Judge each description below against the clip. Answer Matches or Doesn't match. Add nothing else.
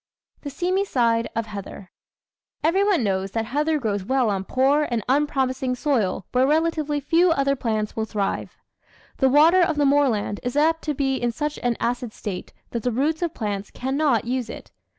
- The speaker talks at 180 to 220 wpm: Matches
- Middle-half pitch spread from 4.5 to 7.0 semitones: Matches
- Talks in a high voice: Matches